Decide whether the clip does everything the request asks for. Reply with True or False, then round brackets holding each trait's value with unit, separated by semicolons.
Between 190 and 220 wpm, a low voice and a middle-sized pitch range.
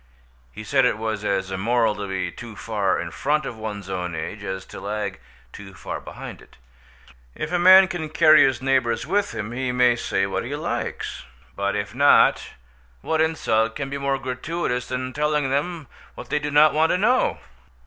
False (195 wpm; 125 Hz; 6.5 semitones)